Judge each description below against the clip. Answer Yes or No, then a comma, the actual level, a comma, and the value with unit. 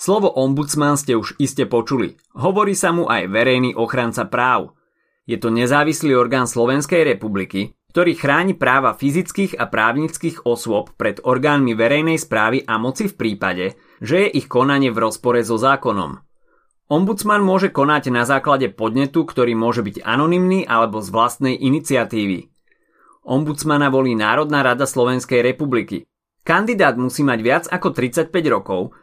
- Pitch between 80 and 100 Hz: No, low, 135 Hz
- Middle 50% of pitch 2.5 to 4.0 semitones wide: No, average, 4.7 semitones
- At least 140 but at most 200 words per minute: Yes, average, 145 wpm